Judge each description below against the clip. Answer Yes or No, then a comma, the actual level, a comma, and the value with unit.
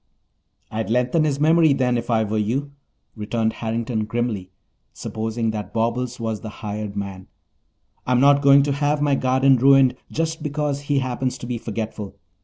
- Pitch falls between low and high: No, low, 125 Hz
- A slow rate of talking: No, average, 165 wpm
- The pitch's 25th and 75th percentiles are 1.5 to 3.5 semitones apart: No, average, 4.0 semitones